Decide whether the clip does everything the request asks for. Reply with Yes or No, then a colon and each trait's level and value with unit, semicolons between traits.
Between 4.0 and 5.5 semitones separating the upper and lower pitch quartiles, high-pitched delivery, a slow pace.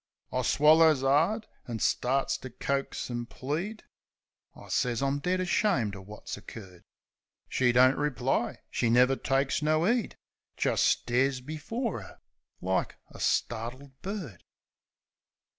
No: average, 4.5 semitones; low, 135 Hz; slow, 125 wpm